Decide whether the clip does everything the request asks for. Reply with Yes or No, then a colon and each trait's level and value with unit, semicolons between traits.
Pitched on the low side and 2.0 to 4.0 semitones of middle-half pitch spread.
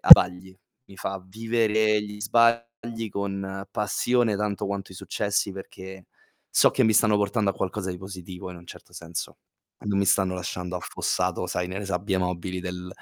Yes: low, 100 Hz; narrow, 2.4 semitones